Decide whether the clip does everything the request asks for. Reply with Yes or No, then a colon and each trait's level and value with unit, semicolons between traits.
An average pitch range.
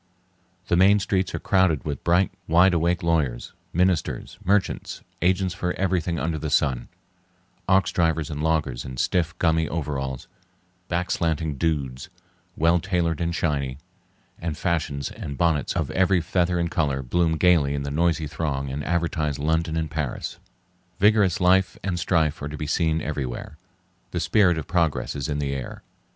Yes: average, 3.2 semitones